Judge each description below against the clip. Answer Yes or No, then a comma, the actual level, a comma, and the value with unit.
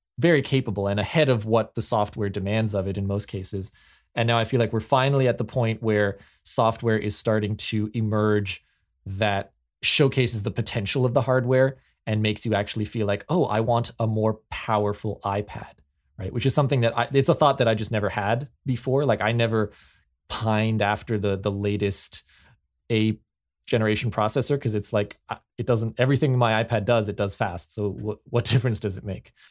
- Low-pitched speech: Yes, low, 110 Hz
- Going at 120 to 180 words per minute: No, average, 195 wpm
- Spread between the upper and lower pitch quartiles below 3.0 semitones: Yes, narrow, 2.6 semitones